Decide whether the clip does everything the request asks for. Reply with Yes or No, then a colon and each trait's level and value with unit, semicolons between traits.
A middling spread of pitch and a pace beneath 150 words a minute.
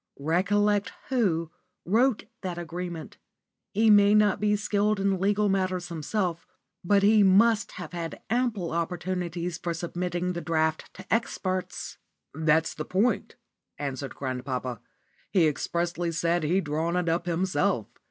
Yes: average, 3.6 semitones; slow, 135 wpm